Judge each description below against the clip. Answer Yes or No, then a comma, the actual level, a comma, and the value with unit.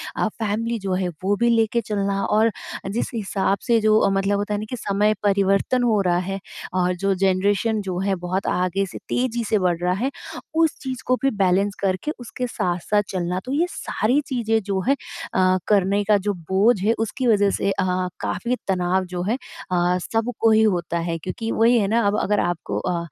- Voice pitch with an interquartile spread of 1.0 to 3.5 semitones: Yes, average, 3.2 semitones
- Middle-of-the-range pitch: No, high, 200 Hz